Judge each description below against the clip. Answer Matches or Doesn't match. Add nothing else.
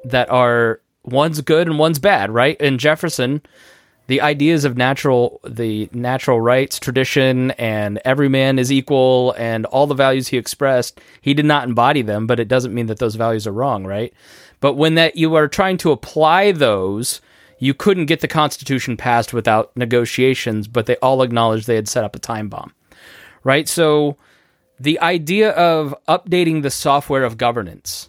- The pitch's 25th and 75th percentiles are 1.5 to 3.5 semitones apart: Doesn't match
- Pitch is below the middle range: Matches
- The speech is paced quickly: Doesn't match